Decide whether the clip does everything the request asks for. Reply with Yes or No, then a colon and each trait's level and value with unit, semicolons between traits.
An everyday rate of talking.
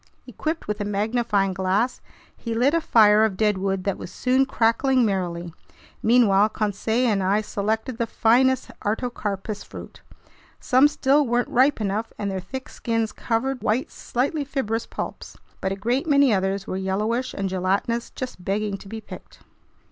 Yes: average, 160 wpm